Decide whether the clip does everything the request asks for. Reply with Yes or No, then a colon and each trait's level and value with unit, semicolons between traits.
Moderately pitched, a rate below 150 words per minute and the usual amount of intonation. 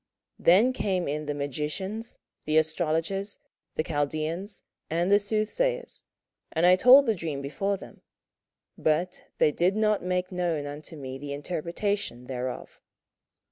Yes: medium, 170 Hz; average, 140 wpm; average, 5.0 semitones